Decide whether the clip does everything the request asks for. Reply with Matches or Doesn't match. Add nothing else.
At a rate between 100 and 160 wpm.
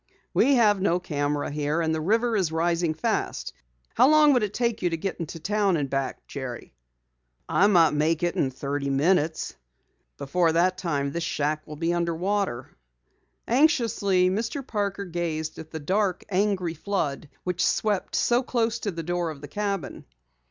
Doesn't match